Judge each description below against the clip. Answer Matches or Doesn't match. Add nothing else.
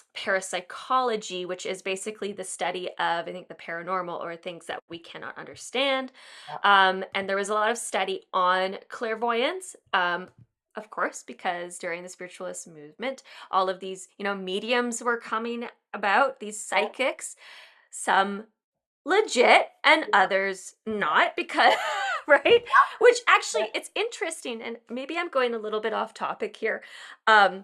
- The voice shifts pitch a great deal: Matches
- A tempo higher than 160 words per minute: Doesn't match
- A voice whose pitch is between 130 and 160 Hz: Doesn't match